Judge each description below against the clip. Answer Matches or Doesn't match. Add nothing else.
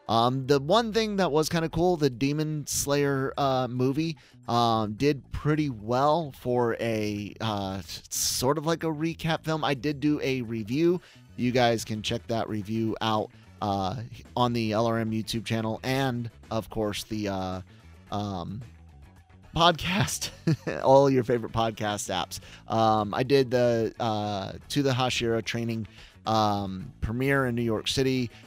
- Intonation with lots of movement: Doesn't match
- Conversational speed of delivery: Matches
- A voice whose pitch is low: Matches